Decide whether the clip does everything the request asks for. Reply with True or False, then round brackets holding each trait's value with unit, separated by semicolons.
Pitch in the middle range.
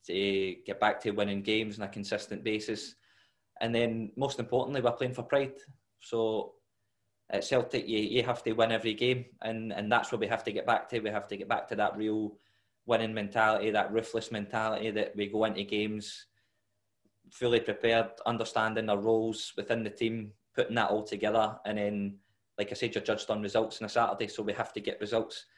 False (110 Hz)